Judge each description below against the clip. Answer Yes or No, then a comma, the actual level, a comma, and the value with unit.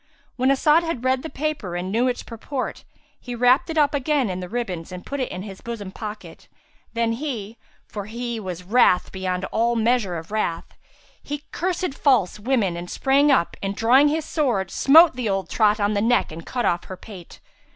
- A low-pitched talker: No, high, 230 Hz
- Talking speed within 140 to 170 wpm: No, average, 195 wpm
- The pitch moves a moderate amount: No, wide, 5.8 semitones